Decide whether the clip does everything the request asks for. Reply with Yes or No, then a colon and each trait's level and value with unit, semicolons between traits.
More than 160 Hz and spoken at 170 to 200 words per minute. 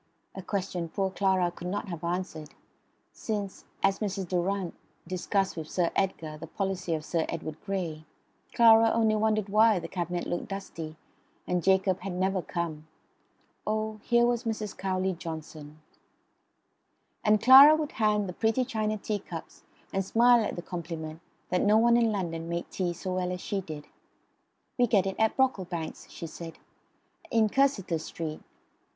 No: high, 190 Hz; average, 160 wpm